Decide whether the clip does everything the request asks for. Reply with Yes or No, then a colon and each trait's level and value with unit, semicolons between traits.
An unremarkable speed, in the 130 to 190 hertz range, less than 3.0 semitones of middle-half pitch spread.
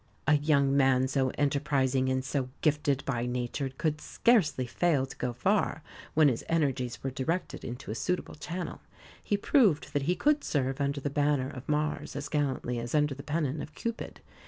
Yes: average, 180 wpm; medium, 140 Hz; narrow, 2.6 semitones